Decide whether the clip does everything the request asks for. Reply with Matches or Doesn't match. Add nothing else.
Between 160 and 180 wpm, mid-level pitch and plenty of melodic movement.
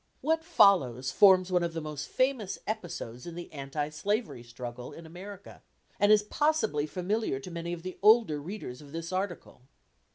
Matches